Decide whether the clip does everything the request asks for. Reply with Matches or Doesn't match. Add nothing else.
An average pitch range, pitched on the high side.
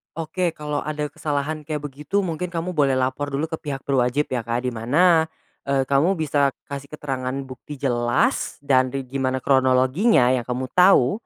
Doesn't match